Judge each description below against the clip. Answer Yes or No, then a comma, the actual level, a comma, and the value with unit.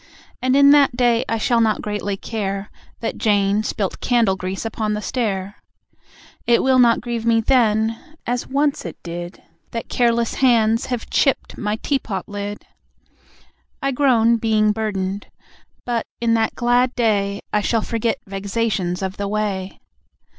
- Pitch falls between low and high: No, high, 225 Hz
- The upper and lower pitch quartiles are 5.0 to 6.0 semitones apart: No, average, 2.9 semitones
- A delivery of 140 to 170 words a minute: Yes, average, 150 wpm